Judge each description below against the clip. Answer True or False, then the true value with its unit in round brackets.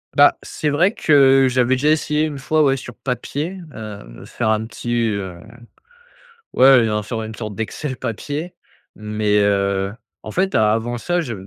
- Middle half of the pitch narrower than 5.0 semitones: False (5.4 semitones)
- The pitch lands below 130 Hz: True (120 Hz)